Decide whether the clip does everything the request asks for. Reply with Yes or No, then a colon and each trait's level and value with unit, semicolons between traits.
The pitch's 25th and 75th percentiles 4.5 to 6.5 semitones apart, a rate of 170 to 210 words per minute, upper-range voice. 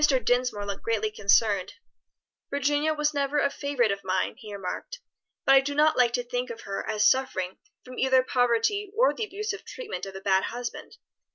Yes: wide, 5.5 semitones; average, 185 wpm; high, 245 Hz